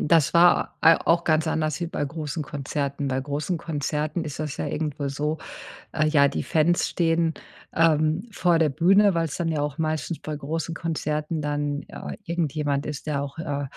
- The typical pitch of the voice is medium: Yes, medium, 155 Hz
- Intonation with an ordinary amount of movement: No, narrow, 2.1 semitones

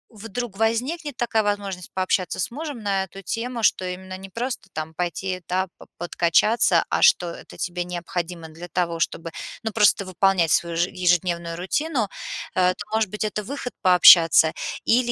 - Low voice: No, high, 190 Hz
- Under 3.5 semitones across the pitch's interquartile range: No, average, 4.1 semitones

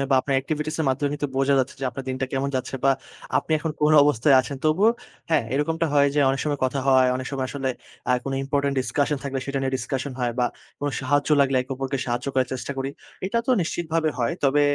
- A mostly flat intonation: Yes, narrow, 2.0 semitones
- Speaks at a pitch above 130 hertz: Yes, medium, 140 Hz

